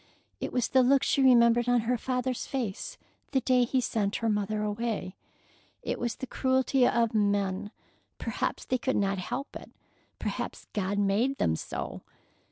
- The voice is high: Yes, high, 235 Hz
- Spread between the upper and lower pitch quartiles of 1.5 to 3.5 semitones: No, average, 3.9 semitones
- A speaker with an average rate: Yes, average, 165 wpm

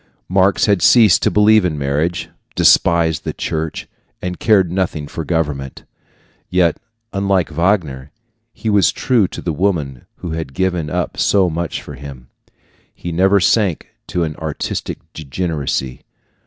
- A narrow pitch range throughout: No, average, 4.1 semitones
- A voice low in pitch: Yes, very low, 85 Hz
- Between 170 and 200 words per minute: No, average, 140 wpm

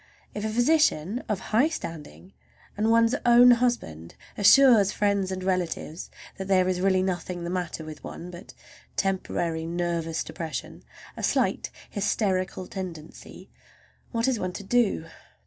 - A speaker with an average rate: No, slow, 130 wpm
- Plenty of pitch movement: No, average, 4.1 semitones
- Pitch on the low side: No, high, 190 Hz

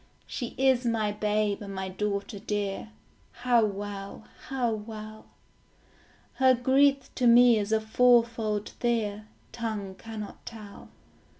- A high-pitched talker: Yes, high, 220 Hz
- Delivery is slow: Yes, slow, 120 wpm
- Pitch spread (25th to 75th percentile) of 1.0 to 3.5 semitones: Yes, narrow, 2.6 semitones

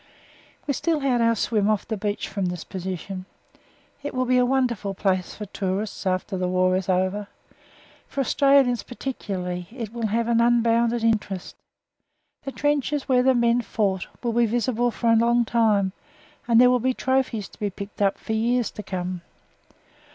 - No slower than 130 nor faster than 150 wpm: No, average, 175 wpm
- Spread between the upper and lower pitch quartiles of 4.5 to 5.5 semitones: No, average, 3.9 semitones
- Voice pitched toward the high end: Yes, high, 225 Hz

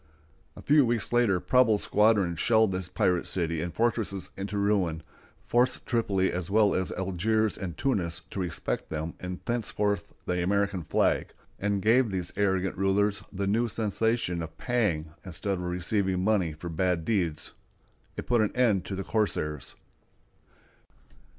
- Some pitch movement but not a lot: Yes, average, 3.7 semitones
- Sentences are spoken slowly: No, average, 150 wpm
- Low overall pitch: Yes, very low, 95 Hz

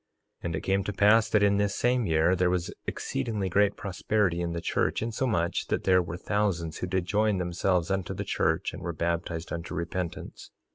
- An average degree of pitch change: Yes, average, 3.2 semitones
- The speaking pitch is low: Yes, very low, 90 Hz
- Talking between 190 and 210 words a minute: Yes, average, 200 wpm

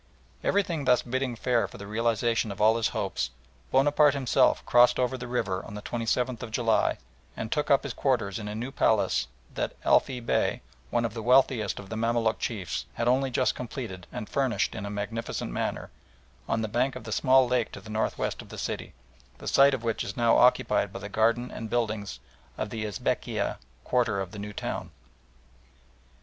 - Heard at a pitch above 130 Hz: No, low, 115 Hz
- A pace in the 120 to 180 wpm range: No, average, 200 wpm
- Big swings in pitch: No, average, 2.8 semitones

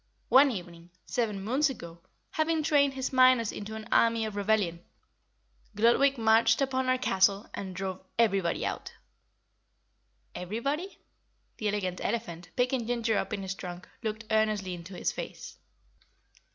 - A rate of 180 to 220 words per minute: No, average, 140 wpm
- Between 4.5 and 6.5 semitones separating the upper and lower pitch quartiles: Yes, average, 4.9 semitones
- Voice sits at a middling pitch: No, high, 220 Hz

